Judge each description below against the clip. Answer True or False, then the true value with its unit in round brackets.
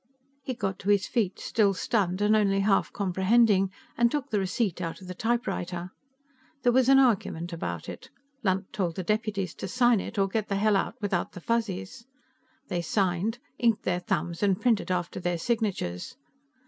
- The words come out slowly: False (180 wpm)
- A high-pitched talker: True (200 Hz)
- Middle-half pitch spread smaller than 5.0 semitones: True (3.7 semitones)